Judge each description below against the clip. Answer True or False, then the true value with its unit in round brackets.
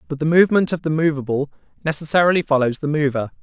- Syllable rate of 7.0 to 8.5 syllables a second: True (7.1 syllables/s)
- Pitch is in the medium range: True (150 Hz)